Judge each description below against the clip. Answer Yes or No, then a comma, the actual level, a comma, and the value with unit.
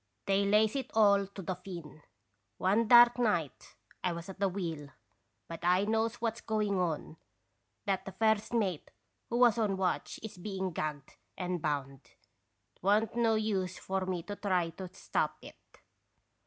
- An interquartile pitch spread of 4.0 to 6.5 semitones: No, average, 3.6 semitones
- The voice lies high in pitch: Yes, high, 195 Hz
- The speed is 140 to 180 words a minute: Yes, average, 170 wpm